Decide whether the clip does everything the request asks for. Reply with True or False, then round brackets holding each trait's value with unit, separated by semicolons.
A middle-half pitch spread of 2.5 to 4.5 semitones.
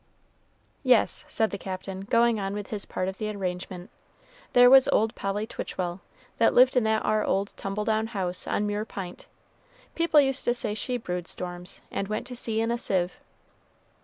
True (3.5 semitones)